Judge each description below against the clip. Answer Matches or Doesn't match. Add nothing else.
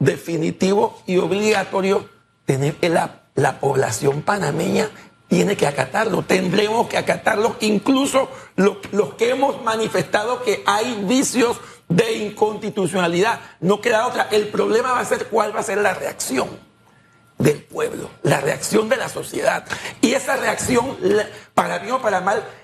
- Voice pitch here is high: Matches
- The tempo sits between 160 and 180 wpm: Doesn't match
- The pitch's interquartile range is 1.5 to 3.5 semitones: Doesn't match